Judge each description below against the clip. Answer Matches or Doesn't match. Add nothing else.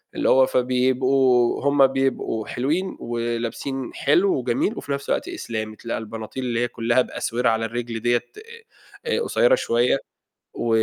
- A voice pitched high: Doesn't match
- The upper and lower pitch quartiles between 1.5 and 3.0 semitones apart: Matches